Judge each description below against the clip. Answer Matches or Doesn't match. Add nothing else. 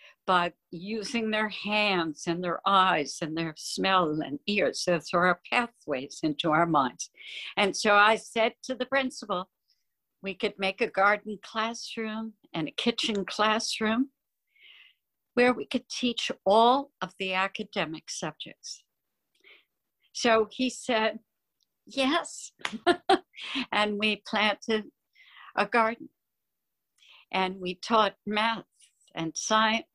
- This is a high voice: Matches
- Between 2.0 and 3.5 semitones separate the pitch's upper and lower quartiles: Doesn't match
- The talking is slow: Matches